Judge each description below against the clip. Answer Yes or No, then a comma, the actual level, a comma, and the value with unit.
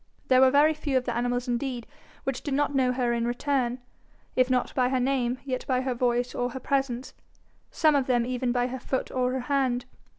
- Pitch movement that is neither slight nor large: No, narrow, 1.6 semitones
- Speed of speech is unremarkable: No, fast, 220 wpm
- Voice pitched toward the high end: Yes, very high, 255 Hz